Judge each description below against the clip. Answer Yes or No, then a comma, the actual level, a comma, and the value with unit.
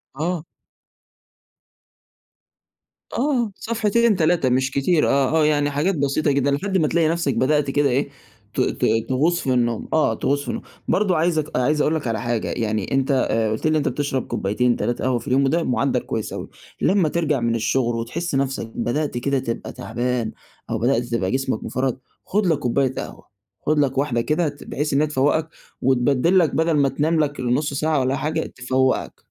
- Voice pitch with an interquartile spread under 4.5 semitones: Yes, average, 3.7 semitones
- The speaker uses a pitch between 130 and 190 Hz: Yes, medium, 140 Hz